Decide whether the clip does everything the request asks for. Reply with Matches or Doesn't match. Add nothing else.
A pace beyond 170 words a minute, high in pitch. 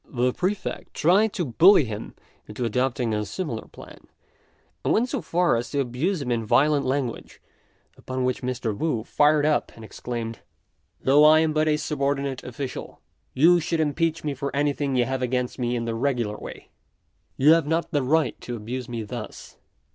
Doesn't match